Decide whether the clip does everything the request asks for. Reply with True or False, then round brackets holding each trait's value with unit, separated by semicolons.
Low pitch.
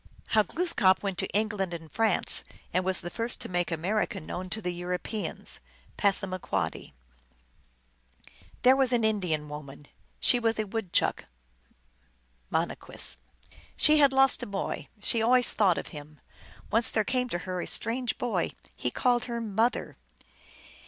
False (205 Hz)